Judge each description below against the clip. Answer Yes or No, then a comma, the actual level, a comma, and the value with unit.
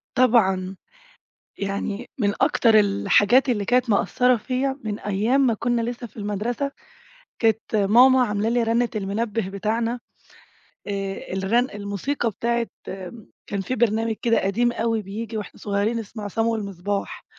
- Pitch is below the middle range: No, high, 220 Hz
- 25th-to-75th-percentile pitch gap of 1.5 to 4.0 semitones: Yes, average, 2.9 semitones